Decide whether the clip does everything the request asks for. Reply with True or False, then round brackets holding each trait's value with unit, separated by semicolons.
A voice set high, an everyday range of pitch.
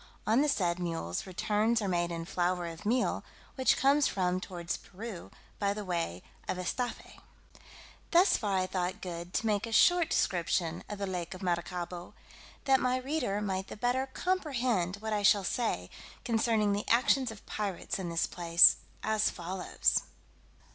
True (200 Hz; 4.7 semitones)